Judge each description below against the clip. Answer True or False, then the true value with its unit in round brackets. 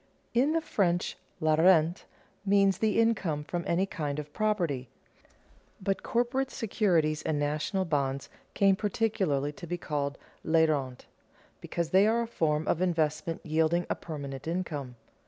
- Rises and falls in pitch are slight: False (4.7 semitones)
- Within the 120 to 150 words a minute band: True (145 wpm)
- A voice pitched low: False (170 Hz)